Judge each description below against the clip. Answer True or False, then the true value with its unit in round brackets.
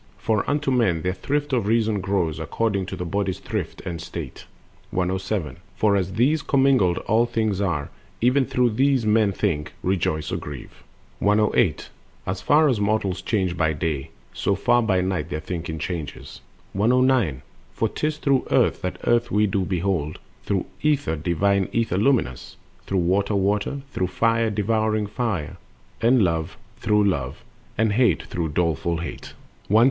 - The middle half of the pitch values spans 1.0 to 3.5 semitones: False (4.6 semitones)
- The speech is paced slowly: False (160 wpm)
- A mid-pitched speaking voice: False (100 Hz)